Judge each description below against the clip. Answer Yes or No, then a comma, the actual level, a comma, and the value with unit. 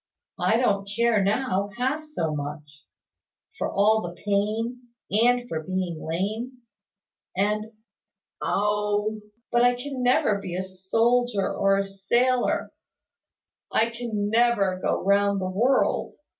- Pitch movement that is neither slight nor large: Yes, average, 3.7 semitones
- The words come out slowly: Yes, slow, 125 wpm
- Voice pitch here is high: Yes, high, 210 Hz